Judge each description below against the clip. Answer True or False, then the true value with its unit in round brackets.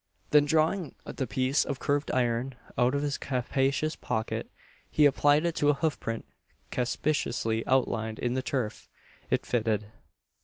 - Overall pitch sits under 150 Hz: True (135 Hz)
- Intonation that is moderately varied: True (3.4 semitones)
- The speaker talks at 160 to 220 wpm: False (150 wpm)